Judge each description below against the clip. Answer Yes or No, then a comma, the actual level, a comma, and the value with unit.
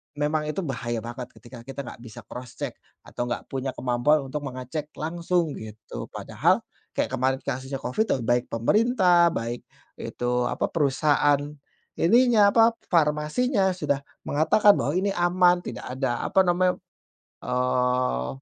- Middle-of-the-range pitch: Yes, medium, 145 Hz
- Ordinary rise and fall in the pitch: No, wide, 6.0 semitones